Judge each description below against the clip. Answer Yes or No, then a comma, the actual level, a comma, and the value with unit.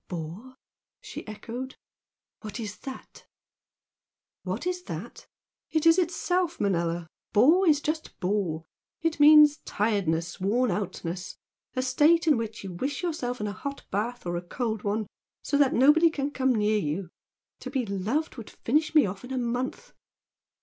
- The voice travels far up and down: Yes, wide, 6.8 semitones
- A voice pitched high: Yes, high, 245 Hz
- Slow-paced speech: No, average, 160 wpm